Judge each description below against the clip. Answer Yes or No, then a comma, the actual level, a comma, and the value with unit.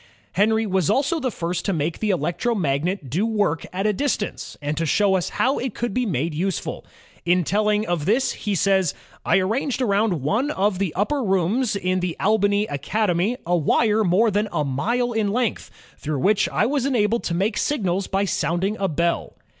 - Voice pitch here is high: Yes, high, 200 Hz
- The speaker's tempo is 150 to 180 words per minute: No, average, 190 wpm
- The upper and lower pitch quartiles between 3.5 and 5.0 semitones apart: Yes, average, 4.1 semitones